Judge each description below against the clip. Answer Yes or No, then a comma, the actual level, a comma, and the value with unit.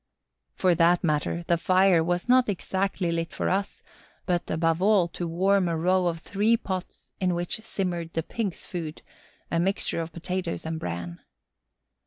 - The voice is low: No, medium, 175 Hz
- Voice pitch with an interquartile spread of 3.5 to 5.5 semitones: No, narrow, 2.4 semitones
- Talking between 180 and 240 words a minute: No, average, 165 wpm